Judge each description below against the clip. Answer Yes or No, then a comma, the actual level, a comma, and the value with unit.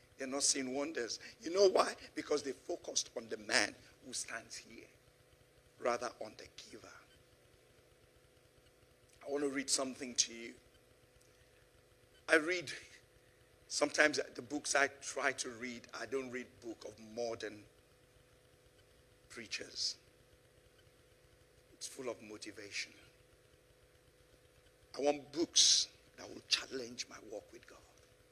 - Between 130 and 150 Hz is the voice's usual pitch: Yes, low, 135 Hz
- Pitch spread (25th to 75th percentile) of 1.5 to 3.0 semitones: Yes, narrow, 2.5 semitones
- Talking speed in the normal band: No, slow, 120 wpm